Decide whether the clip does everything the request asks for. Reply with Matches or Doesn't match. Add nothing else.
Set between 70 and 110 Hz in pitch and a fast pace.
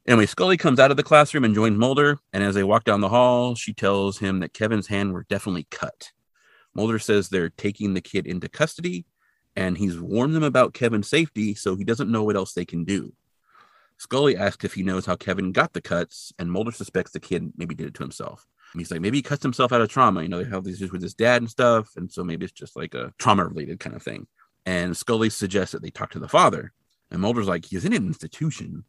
Matches